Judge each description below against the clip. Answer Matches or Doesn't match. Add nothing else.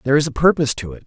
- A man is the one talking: Matches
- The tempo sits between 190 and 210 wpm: Doesn't match